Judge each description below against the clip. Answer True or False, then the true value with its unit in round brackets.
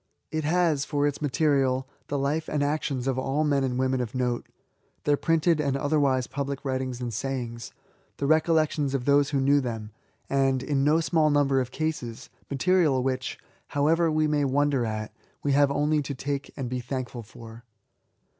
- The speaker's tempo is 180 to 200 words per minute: True (185 wpm)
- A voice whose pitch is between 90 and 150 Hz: True (140 Hz)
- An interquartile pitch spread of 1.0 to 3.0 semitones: True (2.4 semitones)